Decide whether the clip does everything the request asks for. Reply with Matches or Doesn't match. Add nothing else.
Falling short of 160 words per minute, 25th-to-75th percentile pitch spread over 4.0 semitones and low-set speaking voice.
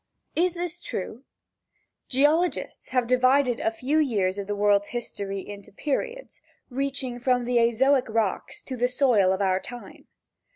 Doesn't match